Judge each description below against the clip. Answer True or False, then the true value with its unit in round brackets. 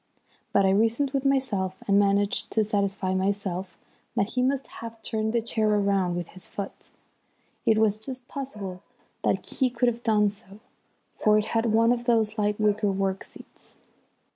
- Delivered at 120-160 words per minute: False (170 wpm)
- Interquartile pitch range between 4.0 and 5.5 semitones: False (2.7 semitones)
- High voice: True (210 Hz)